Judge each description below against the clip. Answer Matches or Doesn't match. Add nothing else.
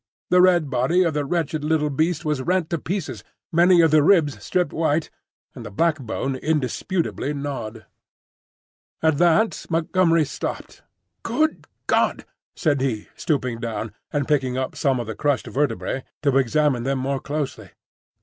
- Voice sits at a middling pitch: Matches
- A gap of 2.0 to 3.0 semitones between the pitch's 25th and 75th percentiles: Doesn't match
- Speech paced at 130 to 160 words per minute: Matches